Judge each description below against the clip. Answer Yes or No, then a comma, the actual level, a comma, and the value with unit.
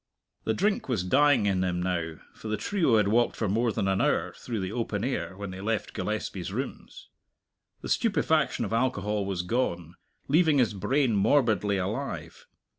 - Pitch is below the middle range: Yes, low, 110 Hz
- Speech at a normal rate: Yes, average, 175 wpm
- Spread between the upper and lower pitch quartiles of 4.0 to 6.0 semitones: Yes, average, 5.2 semitones